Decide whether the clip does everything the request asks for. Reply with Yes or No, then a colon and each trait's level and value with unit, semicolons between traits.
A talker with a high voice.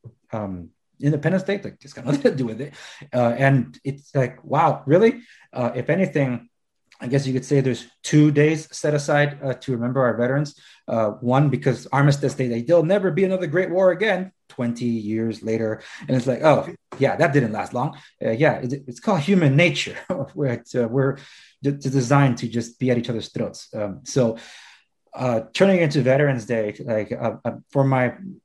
No: low, 135 Hz